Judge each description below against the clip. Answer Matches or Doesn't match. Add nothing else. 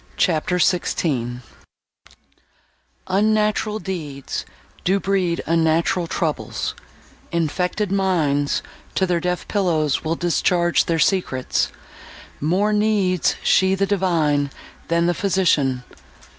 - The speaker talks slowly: Matches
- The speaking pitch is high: Doesn't match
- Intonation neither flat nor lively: Matches